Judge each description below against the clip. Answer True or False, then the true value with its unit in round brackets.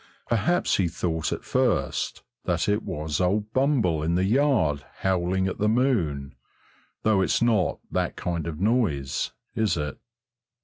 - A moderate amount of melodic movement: False (5.7 semitones)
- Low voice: True (95 Hz)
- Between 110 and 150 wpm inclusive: True (145 wpm)